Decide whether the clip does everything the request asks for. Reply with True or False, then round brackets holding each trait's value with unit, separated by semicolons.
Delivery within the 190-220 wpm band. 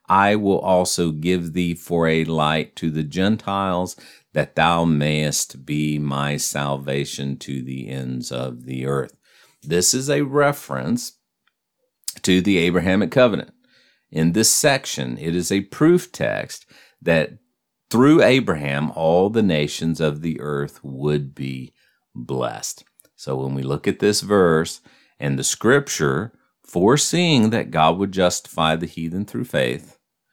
False (140 wpm)